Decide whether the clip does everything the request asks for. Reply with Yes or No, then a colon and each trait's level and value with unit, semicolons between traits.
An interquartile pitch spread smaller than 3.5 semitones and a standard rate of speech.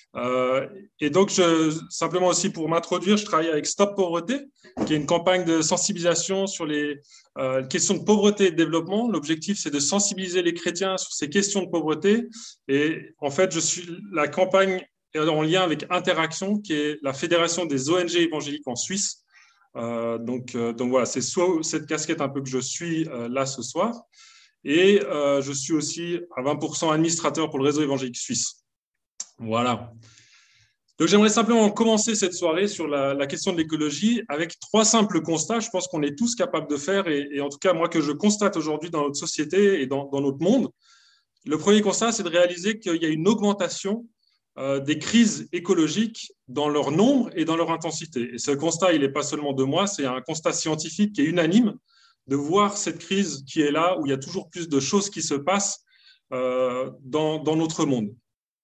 No: average, 5.0 semitones; average, 200 wpm